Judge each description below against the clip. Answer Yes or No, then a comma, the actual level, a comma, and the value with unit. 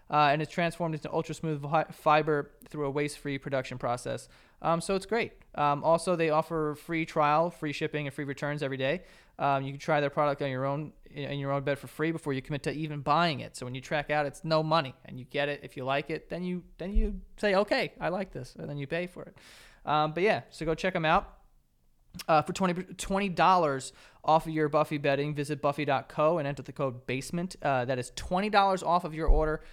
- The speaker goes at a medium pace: No, fast, 235 wpm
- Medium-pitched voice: Yes, medium, 150 Hz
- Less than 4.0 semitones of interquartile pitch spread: Yes, average, 2.8 semitones